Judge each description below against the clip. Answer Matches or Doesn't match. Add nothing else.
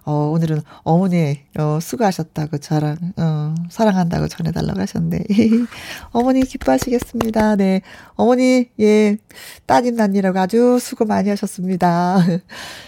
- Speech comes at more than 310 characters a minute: Doesn't match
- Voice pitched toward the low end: Doesn't match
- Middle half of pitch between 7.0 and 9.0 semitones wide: Doesn't match